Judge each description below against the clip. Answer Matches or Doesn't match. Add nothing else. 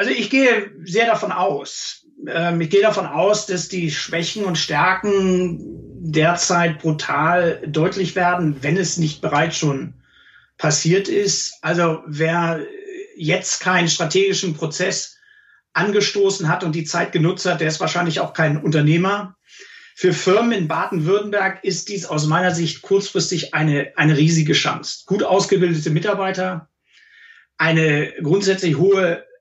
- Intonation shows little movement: Doesn't match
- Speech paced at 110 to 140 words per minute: Matches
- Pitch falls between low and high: Matches